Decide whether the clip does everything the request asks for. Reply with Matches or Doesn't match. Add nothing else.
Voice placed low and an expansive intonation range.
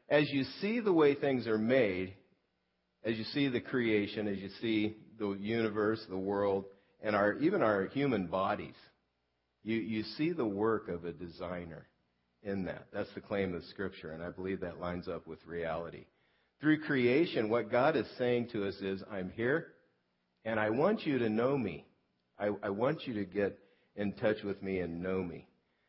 Doesn't match